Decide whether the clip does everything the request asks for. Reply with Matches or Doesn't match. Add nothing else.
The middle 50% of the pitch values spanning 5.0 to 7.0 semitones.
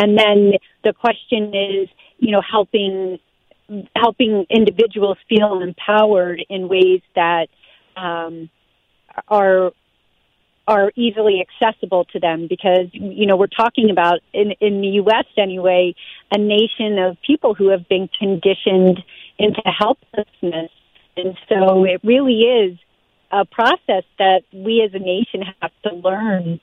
Doesn't match